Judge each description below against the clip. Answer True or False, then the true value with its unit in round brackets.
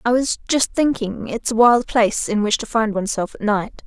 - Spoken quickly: True (250 wpm)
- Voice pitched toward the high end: True (225 Hz)